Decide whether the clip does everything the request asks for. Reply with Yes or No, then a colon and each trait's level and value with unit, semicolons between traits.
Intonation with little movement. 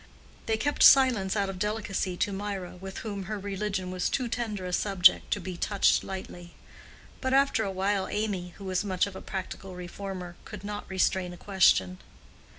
Yes: narrow, 2.1 semitones